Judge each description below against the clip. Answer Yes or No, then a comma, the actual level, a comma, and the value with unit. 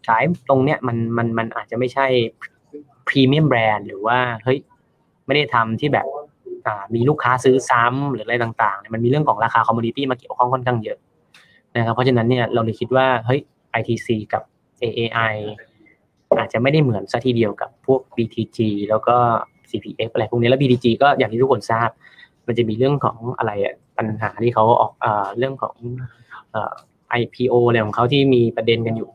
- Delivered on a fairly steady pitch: Yes, narrow, 2.3 semitones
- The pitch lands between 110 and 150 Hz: Yes, low, 120 Hz